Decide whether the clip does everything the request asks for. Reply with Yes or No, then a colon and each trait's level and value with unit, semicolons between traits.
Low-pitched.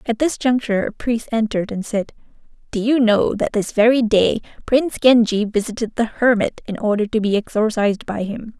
No: high, 220 Hz